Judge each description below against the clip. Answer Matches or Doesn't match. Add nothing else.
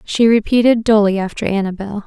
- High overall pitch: Matches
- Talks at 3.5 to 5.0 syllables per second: Doesn't match